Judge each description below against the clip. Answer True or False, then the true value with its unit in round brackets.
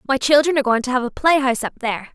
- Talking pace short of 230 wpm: False (310 wpm)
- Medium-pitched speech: False (260 Hz)